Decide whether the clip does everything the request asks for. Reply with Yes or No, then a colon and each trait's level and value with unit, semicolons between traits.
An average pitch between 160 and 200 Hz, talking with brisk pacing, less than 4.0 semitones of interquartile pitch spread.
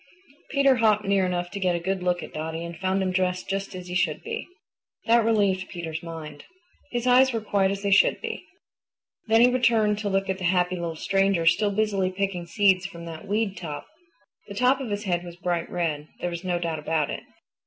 Yes: high, 190 Hz; fast, 215 wpm; average, 3.0 semitones